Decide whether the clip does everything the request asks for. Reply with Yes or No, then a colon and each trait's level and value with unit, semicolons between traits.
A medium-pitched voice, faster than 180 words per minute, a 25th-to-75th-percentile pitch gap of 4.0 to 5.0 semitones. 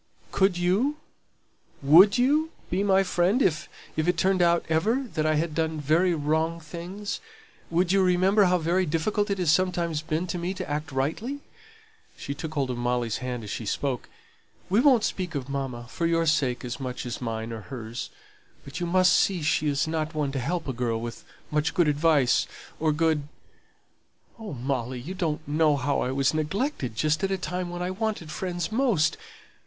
Yes: medium, 160 Hz; average, 190 wpm; average, 4.7 semitones